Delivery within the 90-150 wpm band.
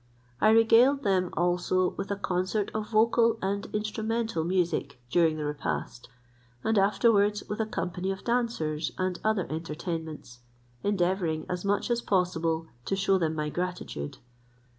Yes: average, 140 wpm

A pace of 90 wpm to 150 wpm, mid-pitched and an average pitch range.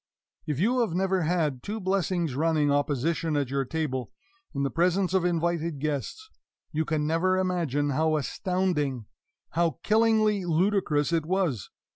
Yes: average, 145 wpm; medium, 165 Hz; average, 4.2 semitones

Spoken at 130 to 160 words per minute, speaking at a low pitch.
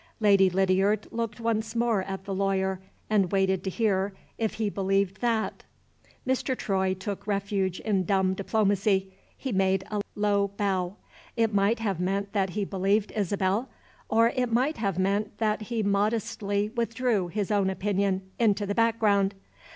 No: average, 155 wpm; high, 200 Hz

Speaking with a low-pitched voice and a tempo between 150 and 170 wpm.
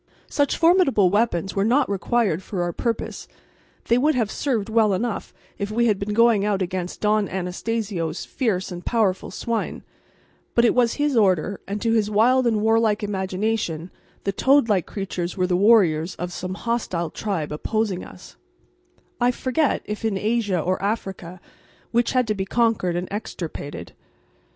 No: high, 210 Hz; average, 165 wpm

